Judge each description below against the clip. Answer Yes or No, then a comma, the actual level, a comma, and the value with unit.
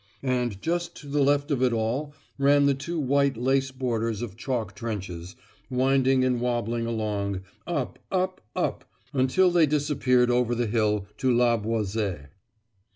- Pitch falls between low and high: No, low, 125 Hz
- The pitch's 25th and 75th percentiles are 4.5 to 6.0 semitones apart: No, average, 3.8 semitones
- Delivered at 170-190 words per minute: No, average, 155 wpm